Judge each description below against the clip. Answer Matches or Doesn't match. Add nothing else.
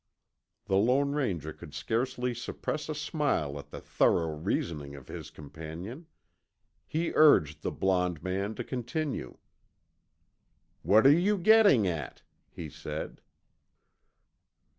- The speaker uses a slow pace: Matches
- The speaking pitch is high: Doesn't match